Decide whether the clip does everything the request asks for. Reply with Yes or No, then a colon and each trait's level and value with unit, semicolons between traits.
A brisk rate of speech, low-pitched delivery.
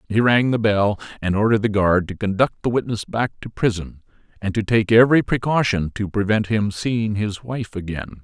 No: average, 195 wpm; low, 105 Hz